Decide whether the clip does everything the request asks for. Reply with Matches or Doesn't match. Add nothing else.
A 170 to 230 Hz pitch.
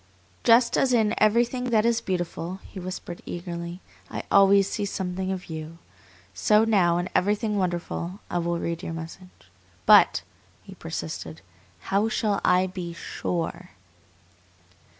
Matches